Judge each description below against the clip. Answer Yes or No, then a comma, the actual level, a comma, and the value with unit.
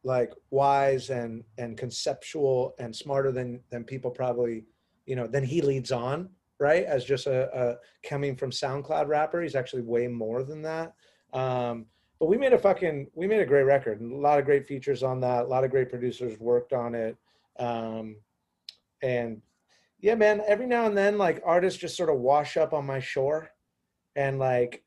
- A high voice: No, low, 130 Hz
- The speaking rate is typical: Yes, average, 190 wpm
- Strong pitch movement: No, average, 3.2 semitones